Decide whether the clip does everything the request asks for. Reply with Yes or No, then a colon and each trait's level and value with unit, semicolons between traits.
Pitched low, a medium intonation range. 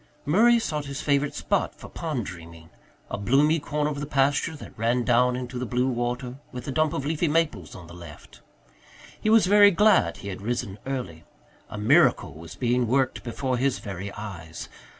No: low, 125 Hz; wide, 6.3 semitones